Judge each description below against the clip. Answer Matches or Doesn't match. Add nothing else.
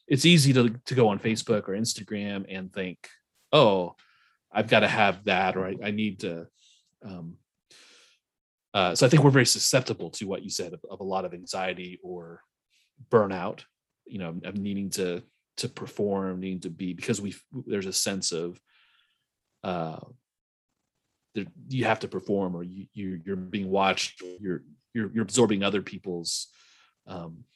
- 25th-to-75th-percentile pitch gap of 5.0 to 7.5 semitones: Doesn't match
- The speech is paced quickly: Doesn't match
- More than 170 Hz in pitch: Doesn't match